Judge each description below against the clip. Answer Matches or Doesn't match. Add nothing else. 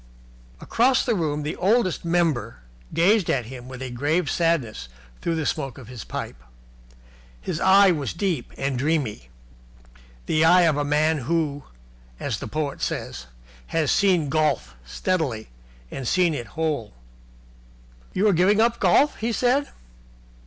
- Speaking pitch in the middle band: Matches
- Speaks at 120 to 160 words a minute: Matches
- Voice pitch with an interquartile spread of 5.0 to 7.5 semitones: Matches